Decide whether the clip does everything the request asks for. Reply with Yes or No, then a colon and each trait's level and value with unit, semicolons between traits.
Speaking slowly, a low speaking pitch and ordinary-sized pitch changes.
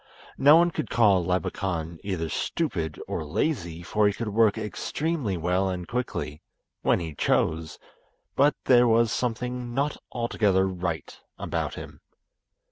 No: slow, 130 wpm; low, 100 Hz; wide, 6.1 semitones